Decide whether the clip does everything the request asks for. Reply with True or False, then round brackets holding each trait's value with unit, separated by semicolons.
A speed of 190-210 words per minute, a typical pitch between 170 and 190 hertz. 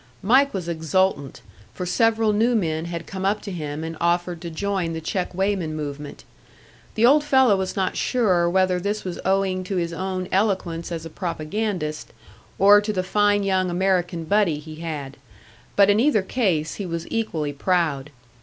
False (175 wpm; 185 Hz)